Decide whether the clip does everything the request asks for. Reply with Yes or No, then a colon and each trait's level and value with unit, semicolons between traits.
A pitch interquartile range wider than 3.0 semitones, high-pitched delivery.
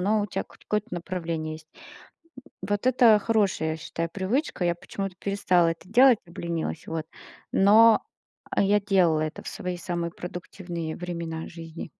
No: average, 3.5 semitones; medium, 180 Hz